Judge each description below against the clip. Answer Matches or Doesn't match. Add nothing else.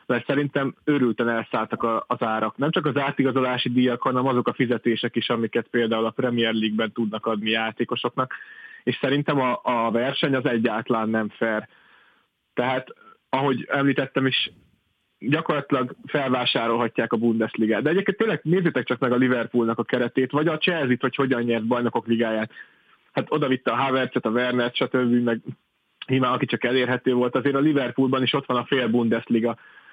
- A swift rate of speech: Matches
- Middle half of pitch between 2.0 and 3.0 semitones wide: Matches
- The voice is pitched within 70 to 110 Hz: Doesn't match